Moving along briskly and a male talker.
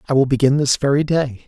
Yes: fast, 245 wpm; male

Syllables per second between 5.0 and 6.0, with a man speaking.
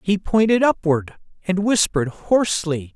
No: 4.6 syllables/s; male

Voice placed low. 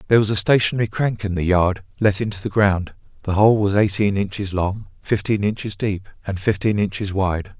Yes: low, 100 Hz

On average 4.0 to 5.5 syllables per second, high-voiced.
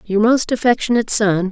No: 5.7 syllables/s; high, 220 Hz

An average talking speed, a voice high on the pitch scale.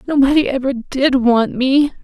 Yes: average, 145 wpm; very high, 265 Hz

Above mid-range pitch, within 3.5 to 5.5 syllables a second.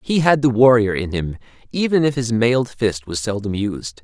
No: low, 115 Hz; 5.0 syllables/s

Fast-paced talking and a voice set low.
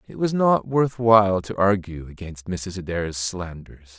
No: average, 165 wpm; very low, 95 Hz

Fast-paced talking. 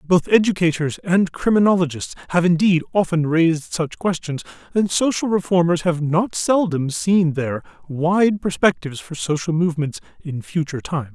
No: average, 140 wpm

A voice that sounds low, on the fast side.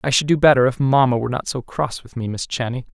Yes: low, 130 Hz; fast, 285 wpm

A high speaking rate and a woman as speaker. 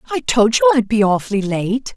Yes: fast, 215 wpm; female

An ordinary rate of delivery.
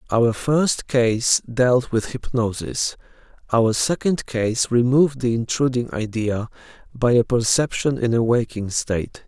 No: slow, 130 wpm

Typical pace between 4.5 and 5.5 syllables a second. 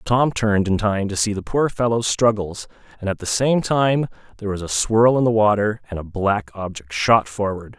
Yes: 5.0 syllables/s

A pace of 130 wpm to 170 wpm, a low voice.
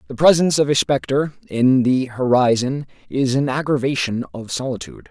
Yes: average, 155 wpm; low, 130 Hz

